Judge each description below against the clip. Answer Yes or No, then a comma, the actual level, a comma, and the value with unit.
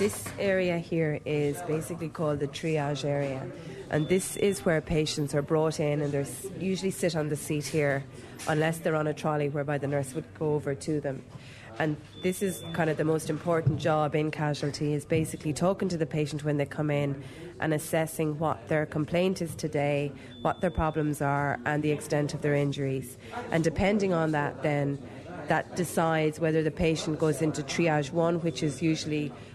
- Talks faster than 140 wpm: Yes, average, 190 wpm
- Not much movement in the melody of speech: Yes, narrow, 2.1 semitones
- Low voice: No, medium, 155 Hz